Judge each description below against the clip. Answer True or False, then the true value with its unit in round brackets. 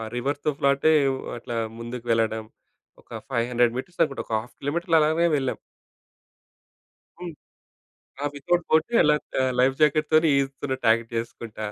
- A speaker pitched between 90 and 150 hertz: True (135 Hz)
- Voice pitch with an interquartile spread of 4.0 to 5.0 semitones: True (4.5 semitones)